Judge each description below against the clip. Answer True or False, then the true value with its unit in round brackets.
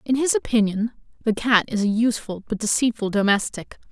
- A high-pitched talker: True (220 Hz)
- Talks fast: False (170 wpm)